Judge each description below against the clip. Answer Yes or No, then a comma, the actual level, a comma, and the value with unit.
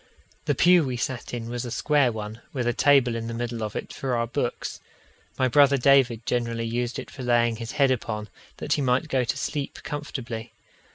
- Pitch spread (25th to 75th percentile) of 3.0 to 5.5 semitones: No, narrow, 2.6 semitones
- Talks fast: Yes, fast, 210 wpm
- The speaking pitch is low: Yes, low, 120 Hz